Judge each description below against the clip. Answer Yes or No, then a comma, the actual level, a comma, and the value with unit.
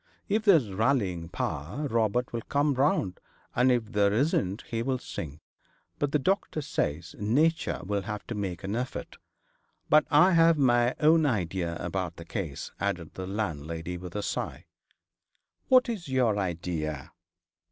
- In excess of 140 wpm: Yes, average, 150 wpm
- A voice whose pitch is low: Yes, low, 110 Hz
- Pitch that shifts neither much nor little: No, wide, 7.8 semitones